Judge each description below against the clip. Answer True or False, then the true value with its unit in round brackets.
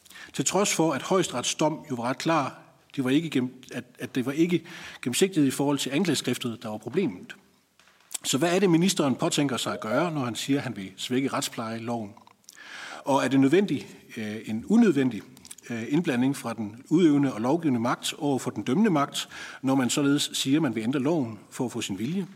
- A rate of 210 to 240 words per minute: False (190 wpm)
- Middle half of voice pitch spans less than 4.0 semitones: False (4.8 semitones)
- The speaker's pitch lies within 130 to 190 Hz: True (135 Hz)